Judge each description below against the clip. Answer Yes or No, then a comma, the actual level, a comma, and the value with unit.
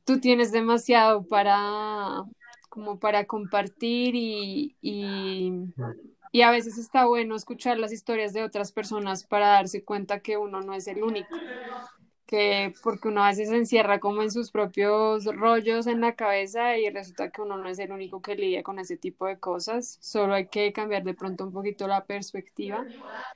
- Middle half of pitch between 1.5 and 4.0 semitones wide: Yes, narrow, 2.6 semitones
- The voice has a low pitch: No, high, 210 Hz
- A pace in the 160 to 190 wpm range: Yes, average, 175 wpm